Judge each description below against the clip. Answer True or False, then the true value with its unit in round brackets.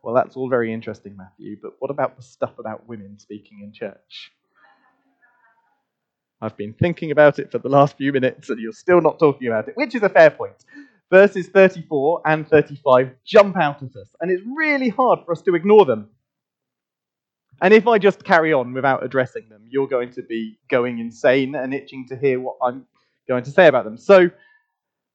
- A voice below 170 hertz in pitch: True (140 Hz)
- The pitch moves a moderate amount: False (7.4 semitones)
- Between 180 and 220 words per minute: True (195 wpm)